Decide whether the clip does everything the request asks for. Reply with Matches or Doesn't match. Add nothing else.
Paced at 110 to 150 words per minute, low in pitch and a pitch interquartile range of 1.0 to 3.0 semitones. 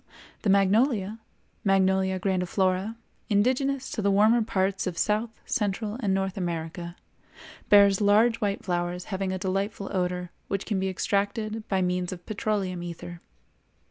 Doesn't match